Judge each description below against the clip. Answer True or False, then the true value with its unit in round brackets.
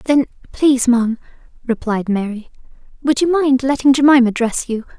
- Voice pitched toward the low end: False (255 Hz)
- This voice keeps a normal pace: True (145 wpm)